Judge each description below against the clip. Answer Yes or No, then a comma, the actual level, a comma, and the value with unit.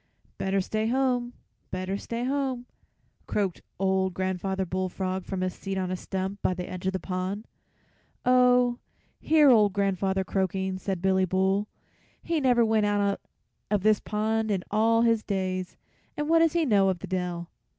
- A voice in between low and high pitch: No, high, 195 Hz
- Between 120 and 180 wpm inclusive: Yes, average, 165 wpm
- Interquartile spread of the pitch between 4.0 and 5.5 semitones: No, average, 3.4 semitones